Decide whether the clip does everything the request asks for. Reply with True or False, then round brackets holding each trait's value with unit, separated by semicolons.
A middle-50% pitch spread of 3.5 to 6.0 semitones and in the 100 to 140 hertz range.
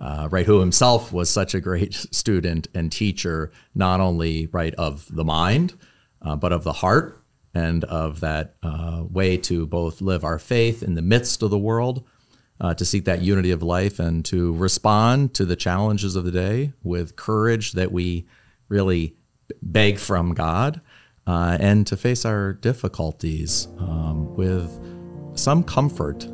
False (4.1 semitones; 90 Hz)